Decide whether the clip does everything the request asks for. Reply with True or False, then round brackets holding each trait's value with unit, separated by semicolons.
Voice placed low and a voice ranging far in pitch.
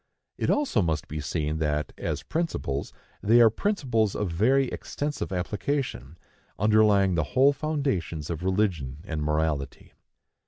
True (95 Hz; 8.5 semitones)